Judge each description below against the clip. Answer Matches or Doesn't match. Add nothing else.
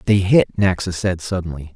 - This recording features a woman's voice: Doesn't match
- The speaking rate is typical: Matches